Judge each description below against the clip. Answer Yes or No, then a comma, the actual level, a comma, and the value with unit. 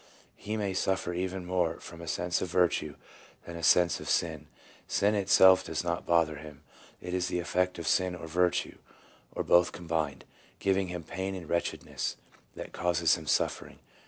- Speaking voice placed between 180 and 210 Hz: No, very low, 90 Hz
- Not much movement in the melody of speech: Yes, narrow, 1.8 semitones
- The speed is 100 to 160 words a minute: No, average, 175 wpm